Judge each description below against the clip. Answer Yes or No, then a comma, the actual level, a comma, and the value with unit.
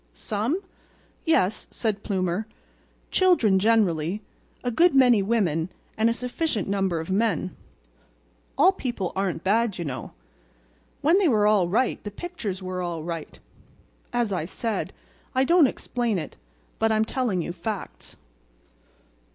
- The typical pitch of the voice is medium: No, high, 210 Hz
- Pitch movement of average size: Yes, average, 4.8 semitones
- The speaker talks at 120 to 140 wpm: Yes, slow, 135 wpm